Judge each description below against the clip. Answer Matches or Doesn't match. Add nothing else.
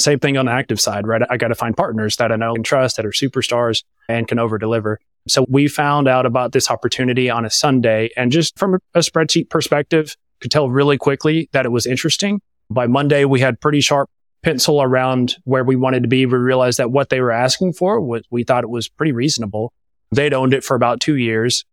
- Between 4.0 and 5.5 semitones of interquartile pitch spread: Doesn't match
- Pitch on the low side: Matches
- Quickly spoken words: Matches